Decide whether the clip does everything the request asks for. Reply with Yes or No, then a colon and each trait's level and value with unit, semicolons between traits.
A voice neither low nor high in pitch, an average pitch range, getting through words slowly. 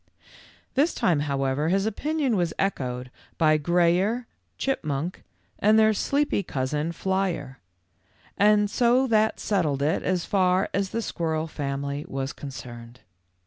No: medium, 170 Hz; wide, 6.6 semitones; slow, 120 wpm